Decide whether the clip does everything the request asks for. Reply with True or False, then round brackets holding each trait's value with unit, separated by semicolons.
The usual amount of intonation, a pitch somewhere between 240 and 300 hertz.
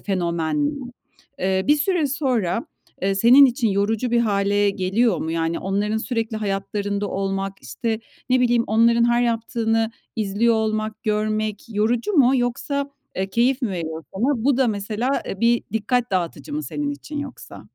False (3.6 semitones; 220 Hz)